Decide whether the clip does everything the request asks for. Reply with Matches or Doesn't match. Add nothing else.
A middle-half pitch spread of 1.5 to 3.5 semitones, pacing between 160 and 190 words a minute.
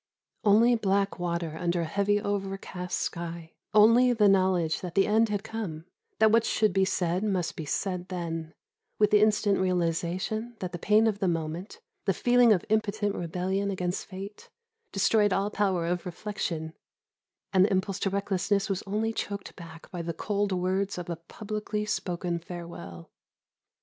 Matches